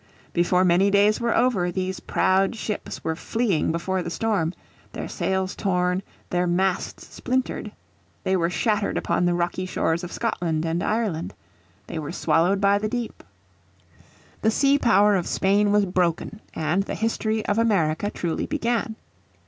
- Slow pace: No, average, 155 wpm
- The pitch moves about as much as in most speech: Yes, average, 3.5 semitones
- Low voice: No, high, 190 Hz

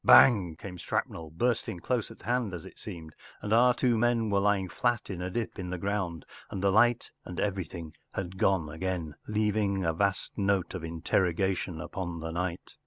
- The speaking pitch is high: No, very low, 95 Hz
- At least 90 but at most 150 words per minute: No, average, 185 wpm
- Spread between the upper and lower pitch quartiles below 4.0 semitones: Yes, average, 3.5 semitones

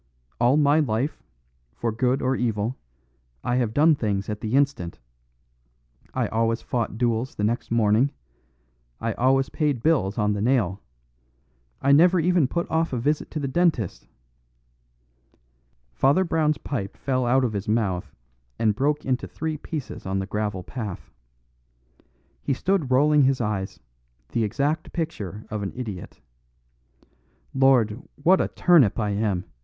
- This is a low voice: Yes, low, 120 Hz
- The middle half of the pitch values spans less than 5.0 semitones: No, wide, 5.4 semitones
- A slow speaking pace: No, average, 150 wpm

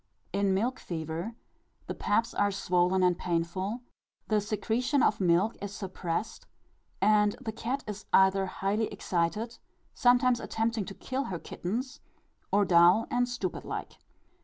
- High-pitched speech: Yes, high, 205 Hz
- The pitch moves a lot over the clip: No, average, 3.8 semitones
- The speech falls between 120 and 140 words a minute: Yes, slow, 135 wpm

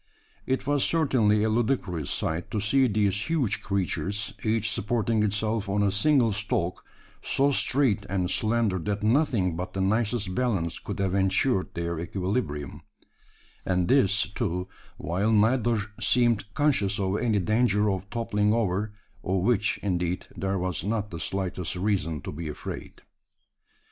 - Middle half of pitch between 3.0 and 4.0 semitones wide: Yes, average, 3.6 semitones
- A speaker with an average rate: Yes, average, 145 wpm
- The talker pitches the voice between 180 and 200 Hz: No, low, 105 Hz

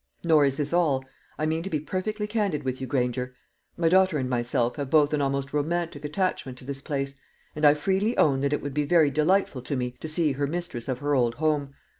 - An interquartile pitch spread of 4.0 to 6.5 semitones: No, average, 3.4 semitones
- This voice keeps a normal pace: No, fast, 230 wpm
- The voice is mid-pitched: Yes, medium, 145 Hz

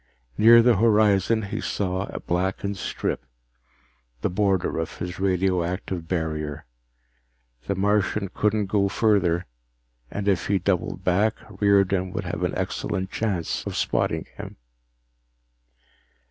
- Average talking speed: No, slow, 120 wpm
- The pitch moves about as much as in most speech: No, narrow, 2.3 semitones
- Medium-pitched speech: No, very low, 95 Hz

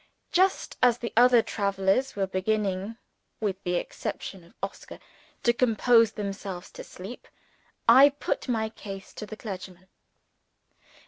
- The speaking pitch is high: Yes, high, 210 Hz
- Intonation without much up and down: No, average, 3.7 semitones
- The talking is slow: Yes, slow, 130 wpm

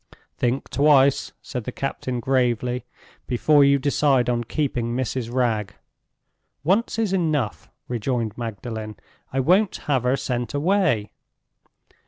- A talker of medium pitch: No, low, 130 Hz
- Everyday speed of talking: No, slow, 120 wpm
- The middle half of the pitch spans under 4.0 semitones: Yes, average, 3.2 semitones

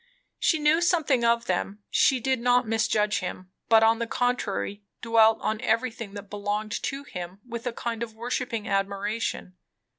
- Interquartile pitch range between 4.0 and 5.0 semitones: No, average, 3.0 semitones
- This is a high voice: Yes, high, 225 Hz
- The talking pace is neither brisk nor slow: Yes, average, 160 wpm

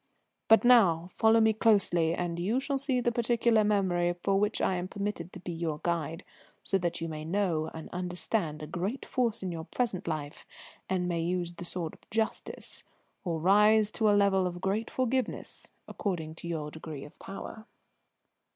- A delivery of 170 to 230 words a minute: Yes, average, 185 wpm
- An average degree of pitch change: Yes, average, 4.5 semitones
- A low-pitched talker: No, medium, 185 Hz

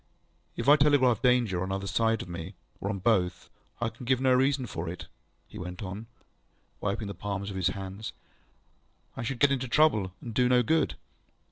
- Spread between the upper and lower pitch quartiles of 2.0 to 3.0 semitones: No, average, 4.7 semitones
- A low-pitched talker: Yes, low, 110 Hz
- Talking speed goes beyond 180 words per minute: Yes, average, 195 wpm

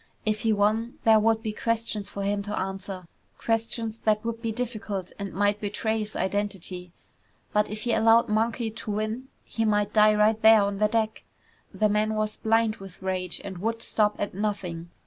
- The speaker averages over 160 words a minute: Yes, average, 185 wpm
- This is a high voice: Yes, high, 215 Hz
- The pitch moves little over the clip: Yes, narrow, 1.8 semitones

